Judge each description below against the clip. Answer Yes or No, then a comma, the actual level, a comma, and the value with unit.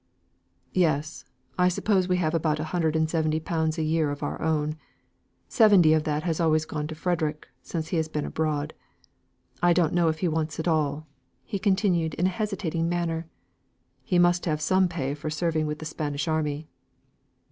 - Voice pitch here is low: No, medium, 160 Hz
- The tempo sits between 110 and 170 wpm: No, average, 185 wpm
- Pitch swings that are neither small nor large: No, narrow, 2.2 semitones